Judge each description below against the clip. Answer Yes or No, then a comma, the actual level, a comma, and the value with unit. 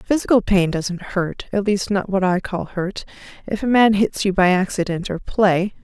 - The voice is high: Yes, high, 195 Hz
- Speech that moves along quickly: No, average, 185 wpm